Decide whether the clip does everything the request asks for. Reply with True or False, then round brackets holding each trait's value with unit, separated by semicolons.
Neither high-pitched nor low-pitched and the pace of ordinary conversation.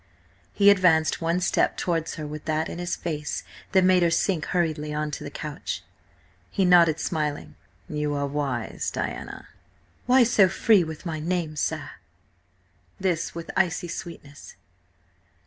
True (165 Hz; 145 wpm)